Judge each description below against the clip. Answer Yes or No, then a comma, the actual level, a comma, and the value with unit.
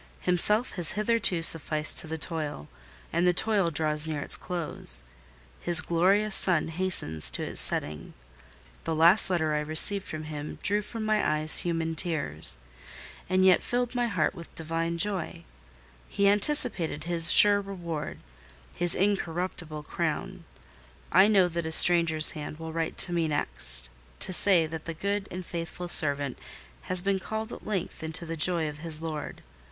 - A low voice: No, medium, 170 Hz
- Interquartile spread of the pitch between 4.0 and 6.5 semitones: No, average, 3.4 semitones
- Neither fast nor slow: Yes, average, 160 wpm